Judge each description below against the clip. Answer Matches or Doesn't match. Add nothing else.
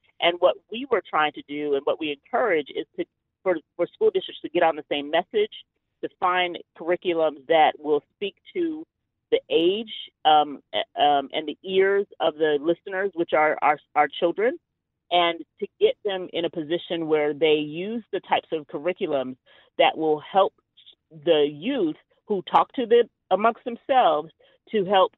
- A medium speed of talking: Matches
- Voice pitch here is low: Doesn't match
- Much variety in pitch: Matches